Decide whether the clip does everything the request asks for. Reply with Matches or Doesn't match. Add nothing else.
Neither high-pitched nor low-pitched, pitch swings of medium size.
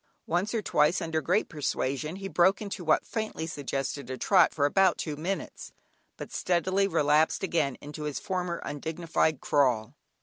Matches